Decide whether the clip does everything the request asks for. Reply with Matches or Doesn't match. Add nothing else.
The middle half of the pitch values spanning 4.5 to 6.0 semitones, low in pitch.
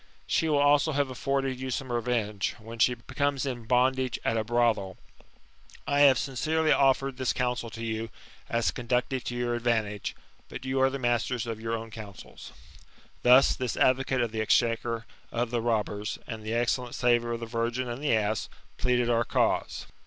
Doesn't match